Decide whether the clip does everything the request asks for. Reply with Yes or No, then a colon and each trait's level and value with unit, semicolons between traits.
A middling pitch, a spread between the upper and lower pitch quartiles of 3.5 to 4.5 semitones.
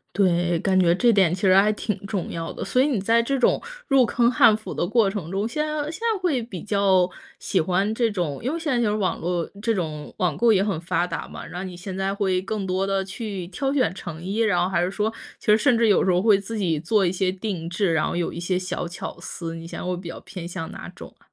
No: high, 195 Hz; average, 3.8 semitones